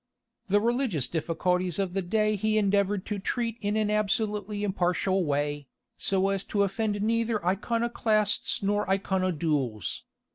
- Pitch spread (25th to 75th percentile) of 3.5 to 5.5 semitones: No, average, 2.8 semitones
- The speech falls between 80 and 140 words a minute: Yes, slow, 135 wpm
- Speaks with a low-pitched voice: No, high, 200 Hz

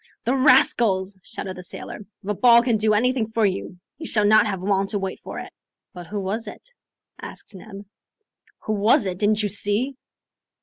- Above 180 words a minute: Yes, average, 190 wpm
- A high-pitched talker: Yes, high, 210 Hz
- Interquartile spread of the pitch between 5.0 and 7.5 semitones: No, average, 3.0 semitones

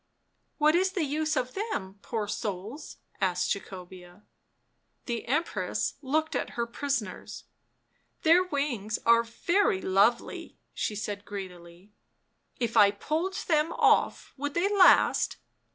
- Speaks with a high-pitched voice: Yes, high, 235 Hz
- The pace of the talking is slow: Yes, slow, 130 wpm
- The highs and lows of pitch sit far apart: Yes, wide, 7.6 semitones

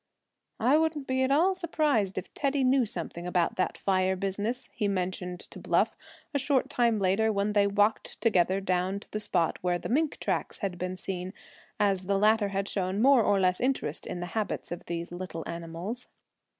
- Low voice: No, high, 200 Hz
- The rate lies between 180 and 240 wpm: Yes, average, 190 wpm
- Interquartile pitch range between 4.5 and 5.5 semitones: Yes, average, 4.8 semitones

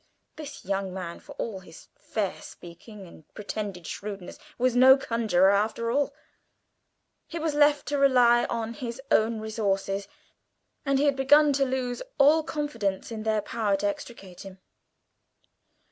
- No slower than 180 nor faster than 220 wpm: No, average, 145 wpm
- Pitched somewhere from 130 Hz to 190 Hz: No, high, 230 Hz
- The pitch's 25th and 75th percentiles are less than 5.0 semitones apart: No, wide, 5.4 semitones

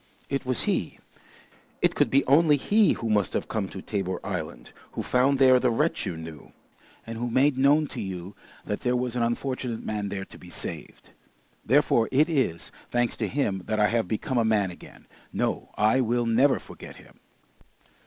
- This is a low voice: Yes, low, 120 Hz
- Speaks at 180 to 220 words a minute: Yes, average, 190 wpm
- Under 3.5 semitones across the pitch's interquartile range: No, average, 4.3 semitones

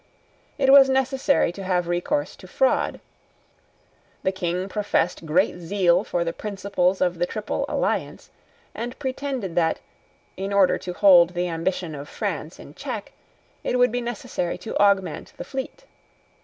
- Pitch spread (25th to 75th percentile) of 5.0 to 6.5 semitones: Yes, wide, 5.6 semitones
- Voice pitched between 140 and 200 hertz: Yes, high, 190 Hz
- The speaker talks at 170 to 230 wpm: No, average, 150 wpm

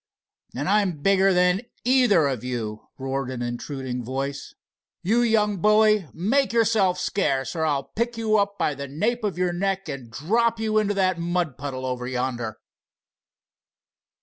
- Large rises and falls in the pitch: Yes, wide, 7.9 semitones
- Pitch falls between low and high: Yes, medium, 180 Hz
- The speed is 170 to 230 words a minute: No, average, 155 wpm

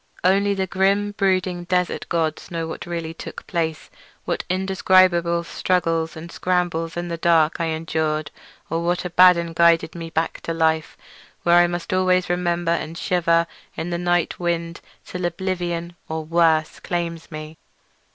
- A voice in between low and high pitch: Yes, medium, 170 Hz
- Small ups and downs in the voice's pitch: Yes, narrow, 1.6 semitones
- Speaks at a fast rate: No, average, 140 wpm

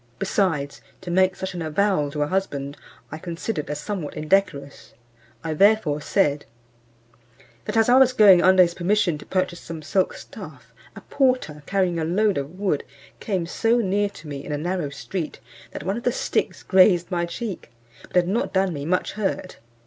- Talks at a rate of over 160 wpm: Yes, average, 185 wpm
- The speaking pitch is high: No, medium, 180 Hz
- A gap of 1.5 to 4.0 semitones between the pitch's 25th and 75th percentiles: No, average, 4.4 semitones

